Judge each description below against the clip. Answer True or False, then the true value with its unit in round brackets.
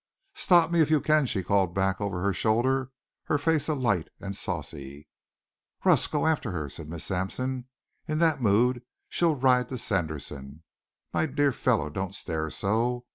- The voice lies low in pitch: True (115 Hz)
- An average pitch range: False (7.6 semitones)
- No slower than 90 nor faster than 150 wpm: False (165 wpm)